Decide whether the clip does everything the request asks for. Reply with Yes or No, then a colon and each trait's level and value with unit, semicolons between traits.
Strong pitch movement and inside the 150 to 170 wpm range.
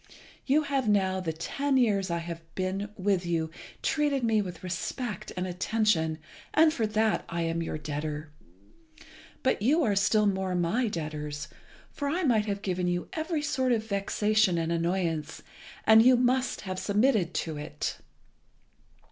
Yes: wide, 5.7 semitones; average, 160 wpm